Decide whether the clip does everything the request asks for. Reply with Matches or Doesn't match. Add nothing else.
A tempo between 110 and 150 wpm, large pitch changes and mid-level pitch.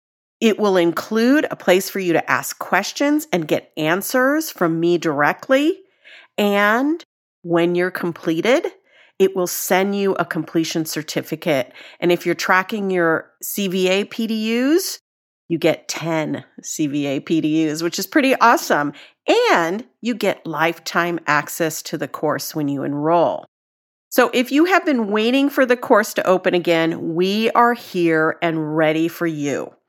Matches